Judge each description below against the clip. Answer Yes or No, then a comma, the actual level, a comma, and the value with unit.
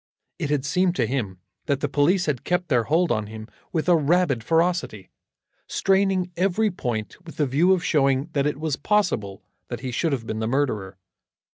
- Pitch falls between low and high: Yes, medium, 145 Hz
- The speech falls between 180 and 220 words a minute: Yes, average, 190 wpm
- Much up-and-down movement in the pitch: Yes, wide, 6.7 semitones